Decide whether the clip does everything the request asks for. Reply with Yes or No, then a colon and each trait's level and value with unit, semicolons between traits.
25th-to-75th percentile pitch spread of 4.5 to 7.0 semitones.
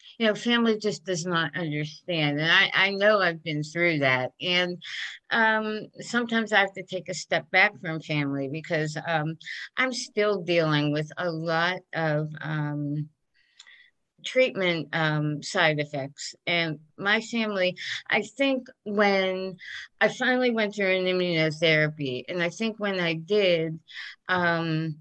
Yes: average, 4.8 semitones